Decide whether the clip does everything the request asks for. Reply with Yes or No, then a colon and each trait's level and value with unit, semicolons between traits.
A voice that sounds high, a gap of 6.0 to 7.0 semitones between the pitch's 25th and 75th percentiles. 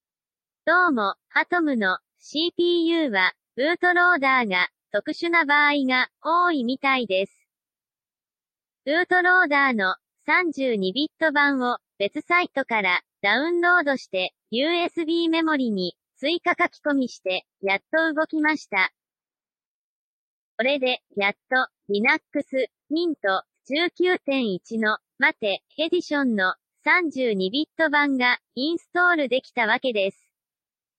Yes: very high, 285 Hz; wide, 6.5 semitones